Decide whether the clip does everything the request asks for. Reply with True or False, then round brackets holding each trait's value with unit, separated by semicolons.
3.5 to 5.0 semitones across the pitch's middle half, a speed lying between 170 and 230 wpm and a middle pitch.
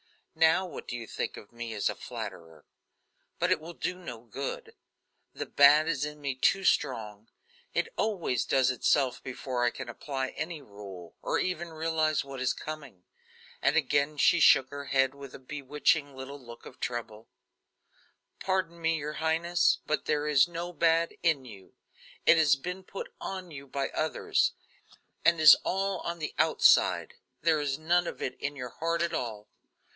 True (4.2 semitones; 175 wpm; 145 Hz)